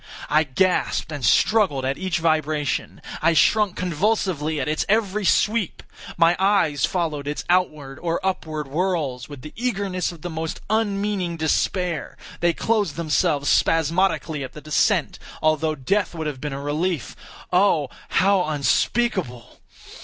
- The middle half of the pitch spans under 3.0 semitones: No, average, 4.2 semitones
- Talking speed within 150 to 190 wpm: No, average, 140 wpm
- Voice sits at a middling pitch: Yes, medium, 165 Hz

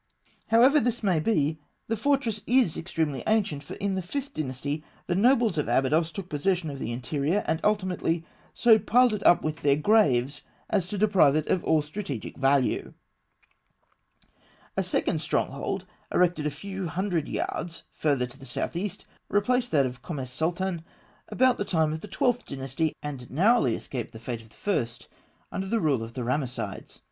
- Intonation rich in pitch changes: Yes, wide, 6.6 semitones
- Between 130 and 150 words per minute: No, average, 175 wpm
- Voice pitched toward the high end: No, medium, 165 Hz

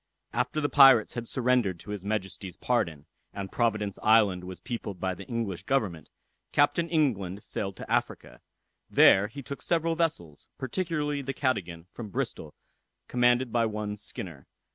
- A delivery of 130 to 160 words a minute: Yes, average, 150 wpm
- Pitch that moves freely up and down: Yes, wide, 5.8 semitones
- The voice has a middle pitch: No, low, 110 Hz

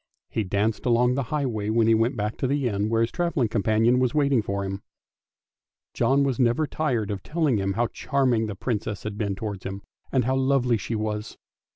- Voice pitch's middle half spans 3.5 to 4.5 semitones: Yes, average, 3.9 semitones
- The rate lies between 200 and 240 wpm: Yes, fast, 205 wpm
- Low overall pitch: Yes, low, 115 Hz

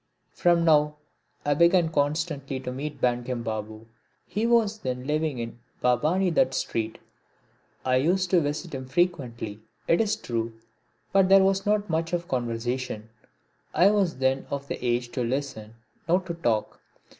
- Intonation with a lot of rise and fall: Yes, wide, 6.0 semitones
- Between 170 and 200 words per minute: No, average, 155 wpm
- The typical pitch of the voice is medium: Yes, medium, 145 Hz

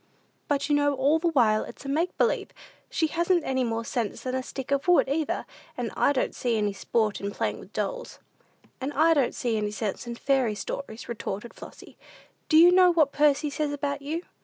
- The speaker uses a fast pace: Yes, fast, 210 wpm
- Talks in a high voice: Yes, very high, 280 Hz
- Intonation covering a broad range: No, average, 4.8 semitones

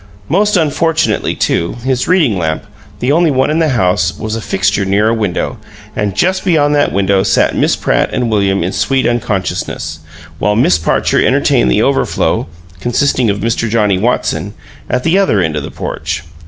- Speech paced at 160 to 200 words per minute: Yes, average, 180 wpm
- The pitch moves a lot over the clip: Yes, wide, 6.9 semitones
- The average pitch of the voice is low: Yes, low, 110 Hz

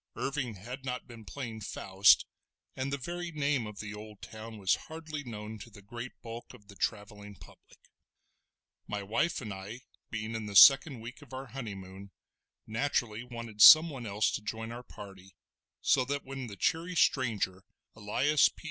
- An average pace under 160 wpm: No, average, 170 wpm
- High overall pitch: No, low, 115 Hz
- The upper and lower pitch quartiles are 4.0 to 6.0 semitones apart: Yes, average, 4.4 semitones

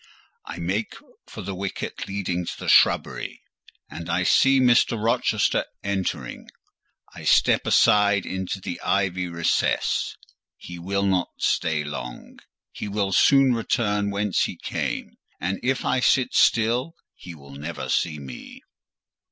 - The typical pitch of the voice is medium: No, very low, 95 Hz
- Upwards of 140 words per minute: No, slow, 135 wpm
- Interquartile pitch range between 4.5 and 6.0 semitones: No, average, 3.6 semitones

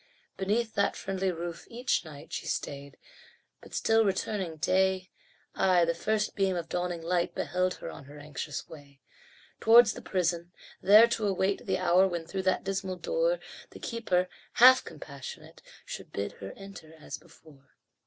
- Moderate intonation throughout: Yes, average, 3.4 semitones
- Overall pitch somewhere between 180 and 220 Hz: Yes, medium, 185 Hz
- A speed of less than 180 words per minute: Yes, average, 160 wpm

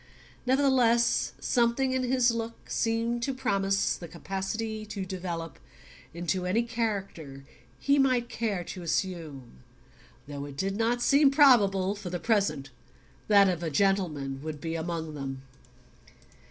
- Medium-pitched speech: No, high, 195 Hz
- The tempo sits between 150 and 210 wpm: No, average, 140 wpm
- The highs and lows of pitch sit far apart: Yes, wide, 6.0 semitones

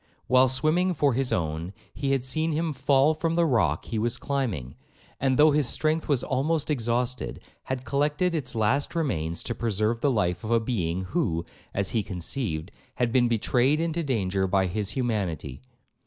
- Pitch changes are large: Yes, wide, 6.3 semitones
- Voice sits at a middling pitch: No, low, 125 Hz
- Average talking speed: Yes, average, 175 wpm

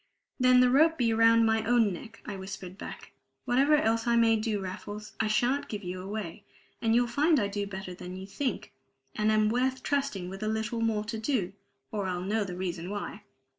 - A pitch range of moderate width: Yes, average, 3.5 semitones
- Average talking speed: No, fast, 210 wpm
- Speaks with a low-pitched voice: No, high, 215 Hz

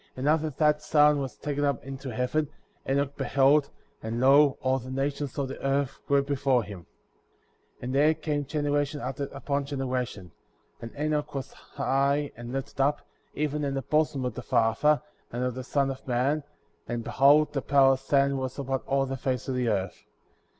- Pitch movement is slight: Yes, narrow, 2.0 semitones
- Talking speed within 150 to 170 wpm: No, average, 190 wpm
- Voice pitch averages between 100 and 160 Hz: Yes, low, 135 Hz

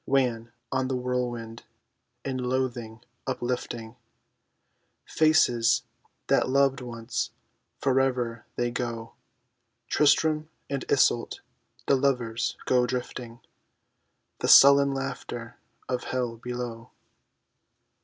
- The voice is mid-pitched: No, low, 125 Hz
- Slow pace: Yes, slow, 90 wpm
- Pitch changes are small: Yes, narrow, 2.2 semitones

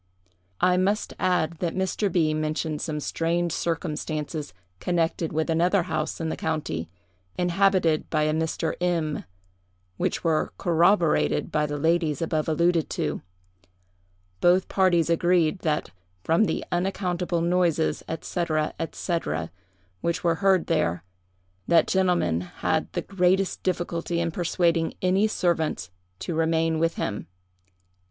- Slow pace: Yes, slow, 125 wpm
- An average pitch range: No, narrow, 2.2 semitones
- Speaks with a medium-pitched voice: Yes, medium, 170 Hz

